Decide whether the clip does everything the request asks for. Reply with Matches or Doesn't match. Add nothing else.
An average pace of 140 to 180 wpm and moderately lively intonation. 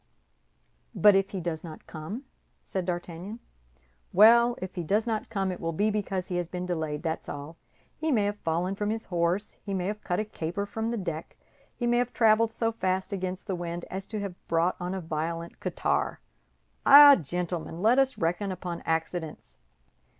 Doesn't match